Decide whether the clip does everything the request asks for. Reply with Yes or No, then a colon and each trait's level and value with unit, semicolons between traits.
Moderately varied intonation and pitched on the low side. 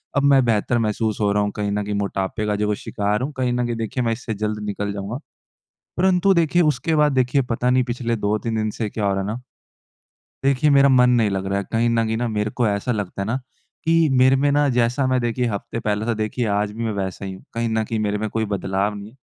Yes: average, 3.5 semitones; low, 115 Hz